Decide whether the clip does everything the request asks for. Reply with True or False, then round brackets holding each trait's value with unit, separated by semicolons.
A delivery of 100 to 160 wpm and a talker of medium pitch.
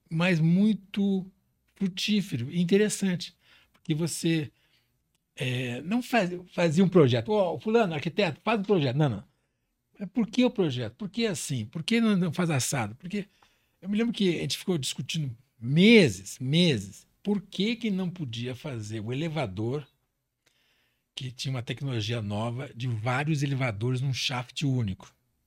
True (155 wpm; 160 Hz)